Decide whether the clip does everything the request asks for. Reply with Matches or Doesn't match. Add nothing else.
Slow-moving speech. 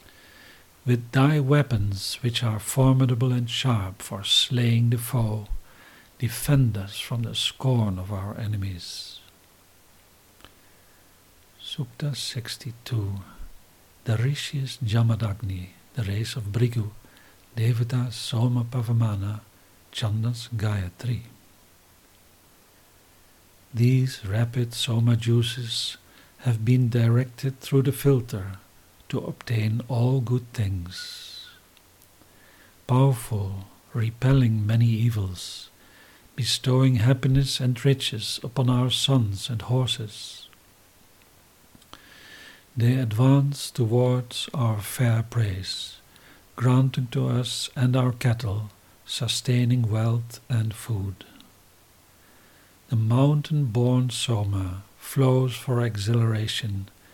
Matches